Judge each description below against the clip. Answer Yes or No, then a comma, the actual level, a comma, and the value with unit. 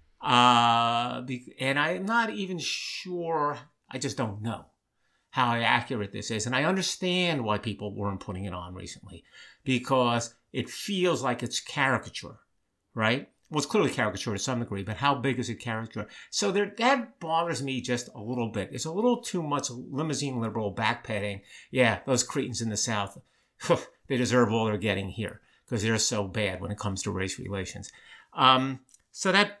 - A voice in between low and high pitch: No, low, 120 Hz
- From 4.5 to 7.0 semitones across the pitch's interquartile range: Yes, average, 5.3 semitones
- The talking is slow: No, average, 170 wpm